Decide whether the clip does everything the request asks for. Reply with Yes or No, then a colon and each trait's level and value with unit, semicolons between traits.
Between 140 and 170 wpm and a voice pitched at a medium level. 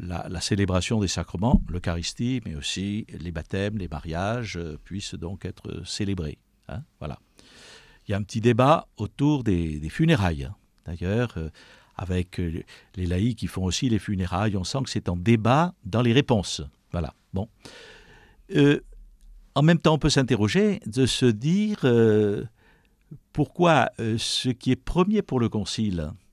No: average, 155 wpm; low, 105 Hz